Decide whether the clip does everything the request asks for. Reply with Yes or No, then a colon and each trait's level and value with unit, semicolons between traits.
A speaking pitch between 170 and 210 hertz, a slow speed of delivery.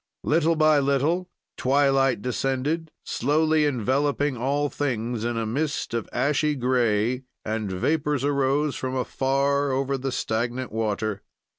No: low, 135 Hz; slow, 125 wpm